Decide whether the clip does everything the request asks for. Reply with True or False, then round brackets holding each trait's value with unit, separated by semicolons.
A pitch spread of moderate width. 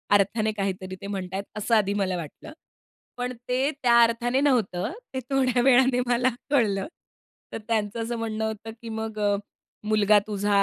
True (3.3 semitones)